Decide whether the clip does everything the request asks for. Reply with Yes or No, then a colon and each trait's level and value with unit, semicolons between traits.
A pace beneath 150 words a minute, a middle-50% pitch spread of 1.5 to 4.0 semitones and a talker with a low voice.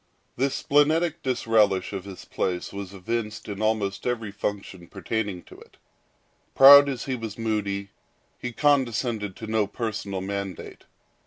Yes: average, 140 wpm; average, 3.7 semitones; low, 110 Hz